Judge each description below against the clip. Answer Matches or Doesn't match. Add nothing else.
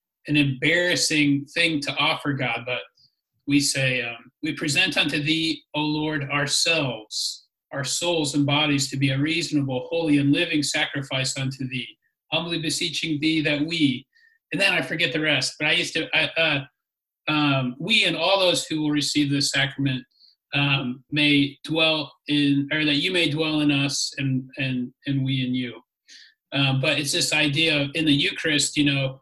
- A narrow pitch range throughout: Matches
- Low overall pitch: Doesn't match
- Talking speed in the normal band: Matches